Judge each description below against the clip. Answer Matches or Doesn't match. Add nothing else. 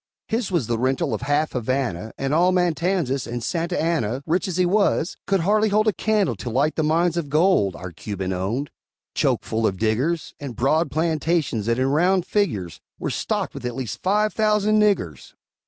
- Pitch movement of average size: Doesn't match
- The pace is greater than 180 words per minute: Matches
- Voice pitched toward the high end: Doesn't match